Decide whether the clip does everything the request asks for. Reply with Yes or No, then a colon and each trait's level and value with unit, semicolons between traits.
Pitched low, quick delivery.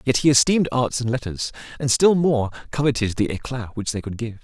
Yes: low, 120 Hz; fast, 215 wpm